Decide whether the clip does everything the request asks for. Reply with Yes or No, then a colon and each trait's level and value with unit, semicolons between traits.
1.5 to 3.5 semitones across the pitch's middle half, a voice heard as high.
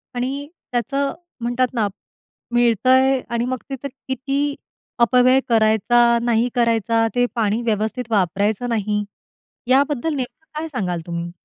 Yes: average, 2.9 semitones; high, 240 Hz